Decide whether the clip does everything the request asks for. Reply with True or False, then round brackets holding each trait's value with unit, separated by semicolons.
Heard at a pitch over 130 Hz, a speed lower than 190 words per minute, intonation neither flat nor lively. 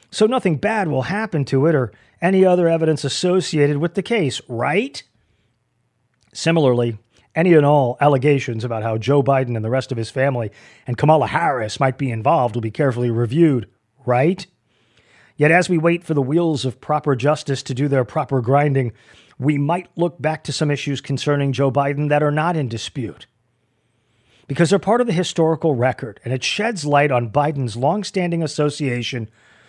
True (140 Hz; 175 wpm; 4.7 semitones)